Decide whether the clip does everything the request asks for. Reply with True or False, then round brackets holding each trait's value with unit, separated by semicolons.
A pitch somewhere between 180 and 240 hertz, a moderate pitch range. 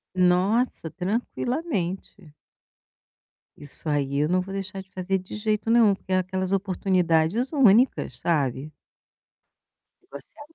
True (190 Hz; 3.8 semitones)